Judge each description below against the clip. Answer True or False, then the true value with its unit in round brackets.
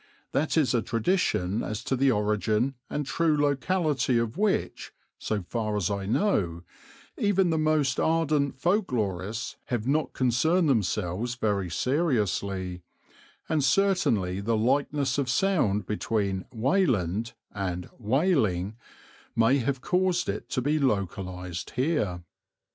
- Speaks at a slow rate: True (125 wpm)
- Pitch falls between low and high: False (120 Hz)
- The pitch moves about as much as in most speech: False (6.8 semitones)